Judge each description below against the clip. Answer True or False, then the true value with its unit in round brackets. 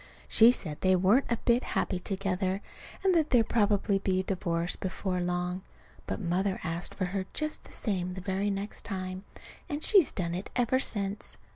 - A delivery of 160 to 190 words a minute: True (180 wpm)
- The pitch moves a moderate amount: True (3.0 semitones)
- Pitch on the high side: True (195 Hz)